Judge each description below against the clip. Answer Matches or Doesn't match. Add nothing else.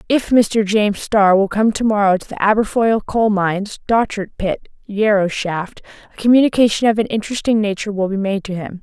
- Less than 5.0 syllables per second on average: Doesn't match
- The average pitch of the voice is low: Doesn't match